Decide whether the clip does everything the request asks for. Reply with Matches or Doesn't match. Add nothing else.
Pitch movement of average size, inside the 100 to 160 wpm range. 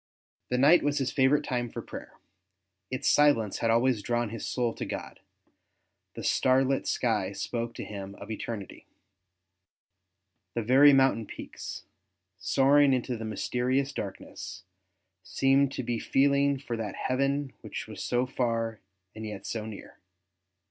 Matches